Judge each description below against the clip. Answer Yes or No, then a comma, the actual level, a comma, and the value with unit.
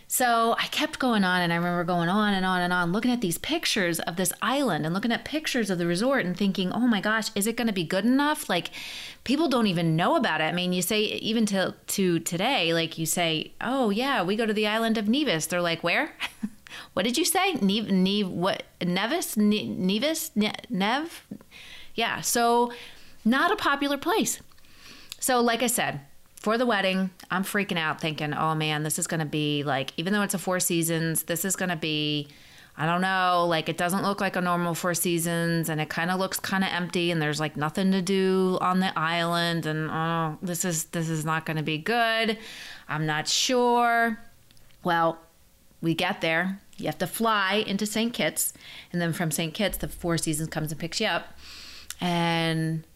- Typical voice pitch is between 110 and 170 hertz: No, medium, 185 Hz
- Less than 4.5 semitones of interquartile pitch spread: No, average, 4.9 semitones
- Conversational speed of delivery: No, fast, 210 wpm